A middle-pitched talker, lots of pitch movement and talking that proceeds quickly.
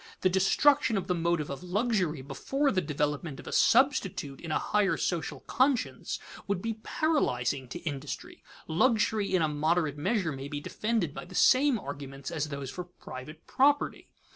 No: medium, 175 Hz; wide, 7.1 semitones; average, 165 wpm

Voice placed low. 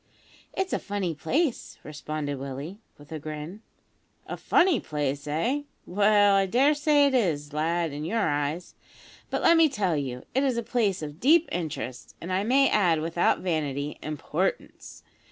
No: medium, 175 Hz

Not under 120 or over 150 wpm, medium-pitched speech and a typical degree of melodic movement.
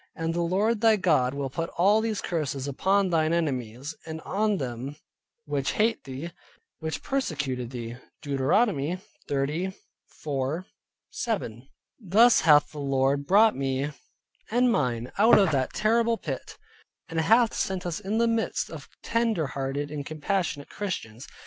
No: average, 145 wpm; medium, 160 Hz; wide, 7.1 semitones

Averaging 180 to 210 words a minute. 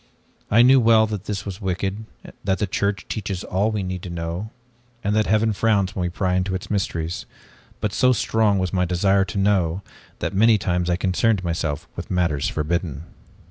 Yes: average, 190 wpm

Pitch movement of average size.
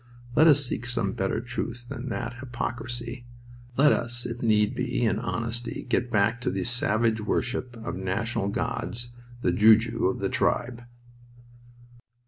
No: narrow, 1.7 semitones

